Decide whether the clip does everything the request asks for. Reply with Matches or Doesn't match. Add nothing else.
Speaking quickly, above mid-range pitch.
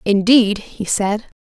Doesn't match